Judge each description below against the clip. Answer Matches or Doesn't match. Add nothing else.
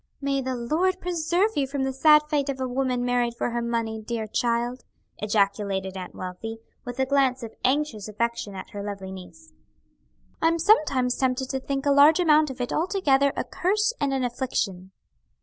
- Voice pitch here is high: Matches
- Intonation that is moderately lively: Matches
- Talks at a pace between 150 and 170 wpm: Doesn't match